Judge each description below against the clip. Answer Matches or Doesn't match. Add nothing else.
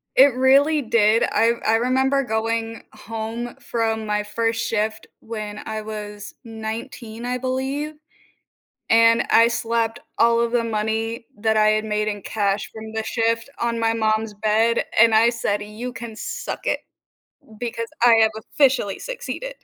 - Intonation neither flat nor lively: Doesn't match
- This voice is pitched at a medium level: Doesn't match